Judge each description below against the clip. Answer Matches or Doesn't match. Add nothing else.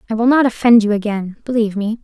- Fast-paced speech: Matches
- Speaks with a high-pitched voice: Matches